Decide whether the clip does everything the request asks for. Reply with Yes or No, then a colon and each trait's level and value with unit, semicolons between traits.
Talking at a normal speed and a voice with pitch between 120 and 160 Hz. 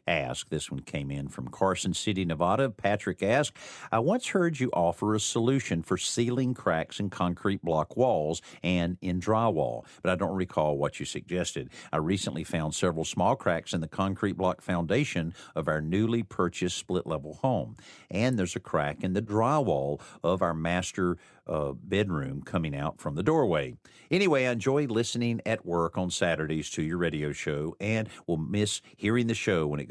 No: average, 180 wpm; very low, 90 Hz